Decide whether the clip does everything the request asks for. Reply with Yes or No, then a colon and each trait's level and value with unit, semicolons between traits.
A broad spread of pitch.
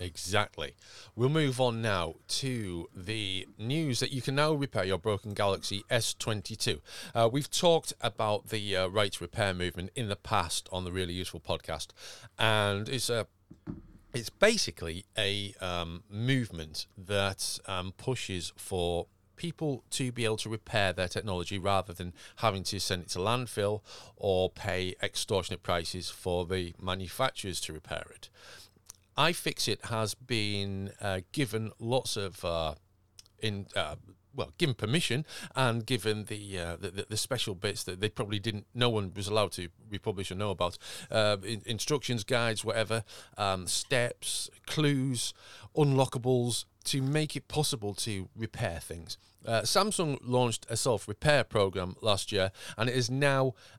No: average, 4.3 semitones